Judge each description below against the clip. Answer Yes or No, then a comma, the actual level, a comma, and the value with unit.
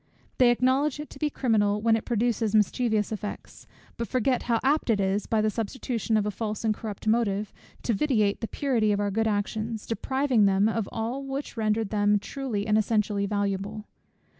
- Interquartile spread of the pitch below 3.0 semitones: Yes, narrow, 2.6 semitones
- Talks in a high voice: Yes, high, 220 Hz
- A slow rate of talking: No, average, 190 wpm